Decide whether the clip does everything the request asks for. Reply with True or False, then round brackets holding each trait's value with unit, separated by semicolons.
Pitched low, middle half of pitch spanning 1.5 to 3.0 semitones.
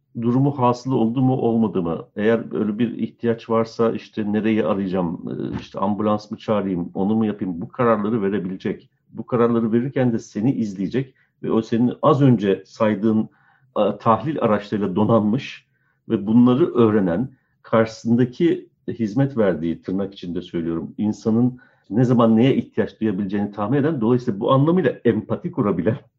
True (115 Hz; 2.7 semitones)